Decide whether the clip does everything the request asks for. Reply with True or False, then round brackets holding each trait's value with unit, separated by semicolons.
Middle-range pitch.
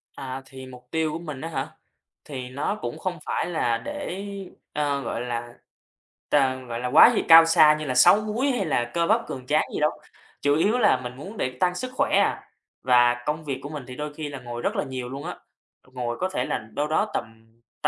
True (145 Hz)